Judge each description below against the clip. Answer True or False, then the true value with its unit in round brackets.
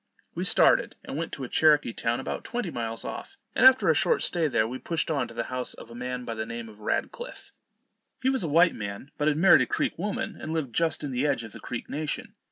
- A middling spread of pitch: False (6.1 semitones)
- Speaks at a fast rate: True (255 wpm)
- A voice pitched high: False (145 Hz)